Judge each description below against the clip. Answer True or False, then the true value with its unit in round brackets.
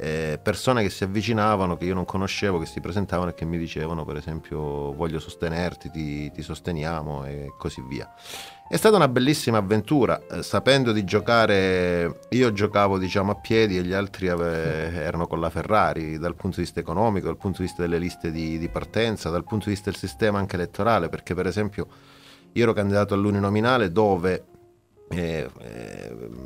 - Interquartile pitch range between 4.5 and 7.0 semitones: False (3.9 semitones)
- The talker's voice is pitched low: True (90 Hz)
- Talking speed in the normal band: False (175 wpm)